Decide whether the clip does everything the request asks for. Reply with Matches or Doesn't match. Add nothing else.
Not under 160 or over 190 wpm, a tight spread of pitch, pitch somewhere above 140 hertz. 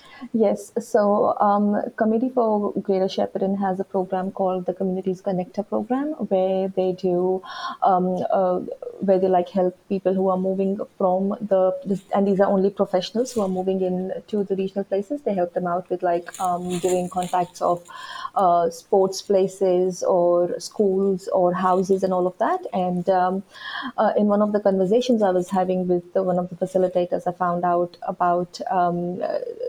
Matches